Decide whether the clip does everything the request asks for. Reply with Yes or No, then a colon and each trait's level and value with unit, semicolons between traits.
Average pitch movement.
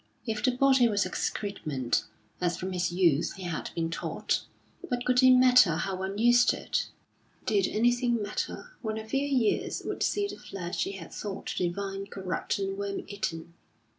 Yes: average, 5.0 semitones